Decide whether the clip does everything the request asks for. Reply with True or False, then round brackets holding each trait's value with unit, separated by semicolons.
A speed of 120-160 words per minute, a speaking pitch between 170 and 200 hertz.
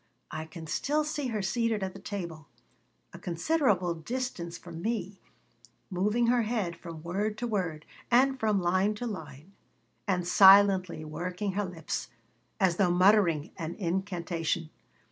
True (145 wpm; 190 Hz)